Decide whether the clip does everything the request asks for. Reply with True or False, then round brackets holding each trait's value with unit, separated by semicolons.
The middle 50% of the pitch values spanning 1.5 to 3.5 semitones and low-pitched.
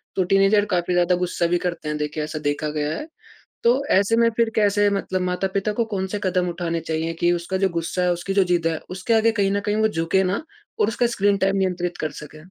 False (3.1 semitones; 185 Hz)